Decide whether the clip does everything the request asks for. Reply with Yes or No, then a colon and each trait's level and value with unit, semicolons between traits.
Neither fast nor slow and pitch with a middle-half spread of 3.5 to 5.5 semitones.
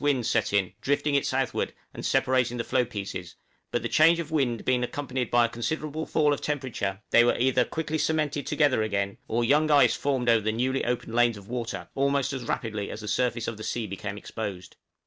No: fast, 210 wpm; average, 4.2 semitones